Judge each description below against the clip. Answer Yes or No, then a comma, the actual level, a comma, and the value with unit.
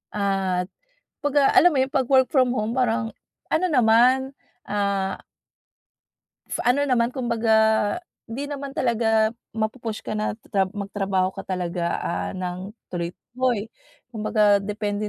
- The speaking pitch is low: No, high, 220 Hz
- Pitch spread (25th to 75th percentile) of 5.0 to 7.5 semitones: No, average, 4.0 semitones